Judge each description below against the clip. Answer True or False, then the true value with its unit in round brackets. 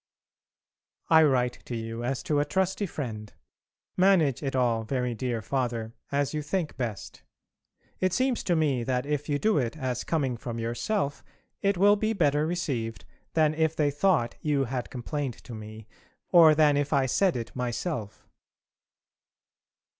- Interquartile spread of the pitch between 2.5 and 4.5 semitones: False (4.9 semitones)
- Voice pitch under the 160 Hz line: True (140 Hz)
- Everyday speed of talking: True (160 wpm)